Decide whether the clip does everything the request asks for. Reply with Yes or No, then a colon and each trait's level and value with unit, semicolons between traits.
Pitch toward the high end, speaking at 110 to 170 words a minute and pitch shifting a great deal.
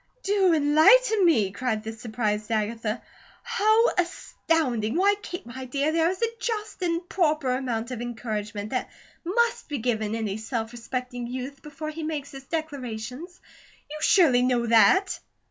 Yes: very high, 260 Hz; average, 150 wpm; wide, 6.7 semitones